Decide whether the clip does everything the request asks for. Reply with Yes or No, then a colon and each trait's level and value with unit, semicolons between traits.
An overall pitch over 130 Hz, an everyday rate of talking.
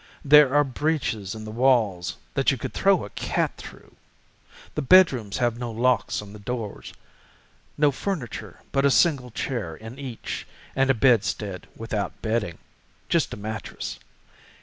No: low, 120 Hz; average, 150 wpm